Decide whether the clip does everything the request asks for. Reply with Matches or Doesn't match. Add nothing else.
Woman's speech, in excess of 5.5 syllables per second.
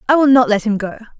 Matches